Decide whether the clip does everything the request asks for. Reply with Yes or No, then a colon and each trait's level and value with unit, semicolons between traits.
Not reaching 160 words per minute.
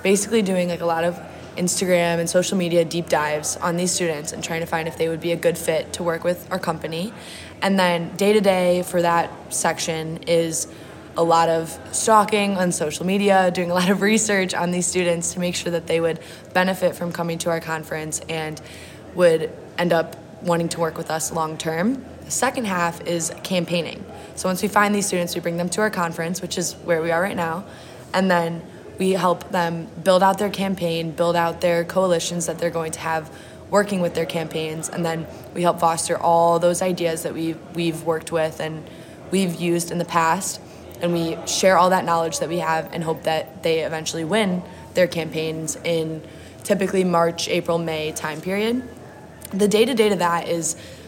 No: fast, 205 wpm